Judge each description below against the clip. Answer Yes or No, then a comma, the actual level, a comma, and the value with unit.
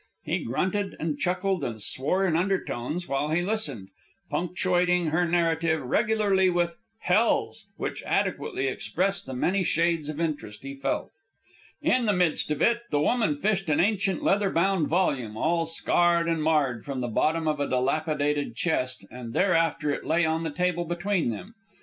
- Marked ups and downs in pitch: No, average, 4.1 semitones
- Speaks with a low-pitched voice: No, medium, 165 Hz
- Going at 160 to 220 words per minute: Yes, average, 165 wpm